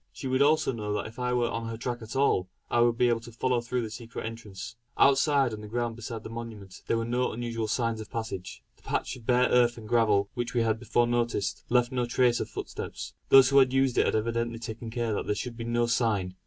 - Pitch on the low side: Yes, low, 115 Hz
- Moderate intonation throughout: No, narrow, 1.7 semitones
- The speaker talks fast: Yes, fast, 250 wpm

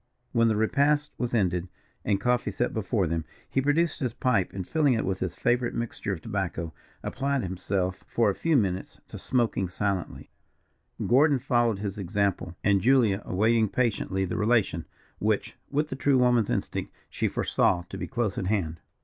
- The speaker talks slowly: No, average, 175 wpm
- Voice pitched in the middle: No, low, 110 Hz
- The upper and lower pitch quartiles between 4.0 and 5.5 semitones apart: Yes, average, 4.7 semitones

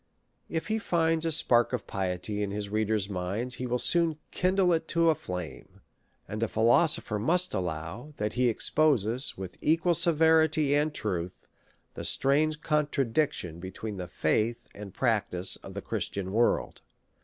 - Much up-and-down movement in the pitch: Yes, wide, 7.8 semitones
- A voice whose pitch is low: Yes, low, 120 Hz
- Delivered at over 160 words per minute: No, average, 155 wpm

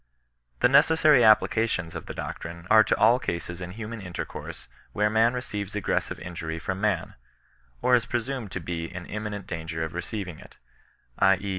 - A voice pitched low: Yes, low, 100 Hz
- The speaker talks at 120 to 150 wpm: No, average, 175 wpm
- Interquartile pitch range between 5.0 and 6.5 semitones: No, average, 4.5 semitones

